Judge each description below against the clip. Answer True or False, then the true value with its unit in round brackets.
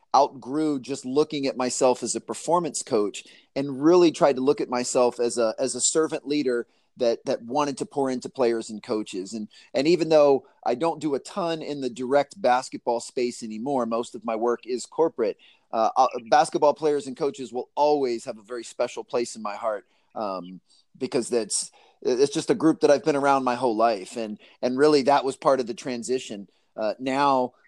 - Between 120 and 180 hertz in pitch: True (135 Hz)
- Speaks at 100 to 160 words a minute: False (200 wpm)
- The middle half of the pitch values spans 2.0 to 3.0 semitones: False (3.7 semitones)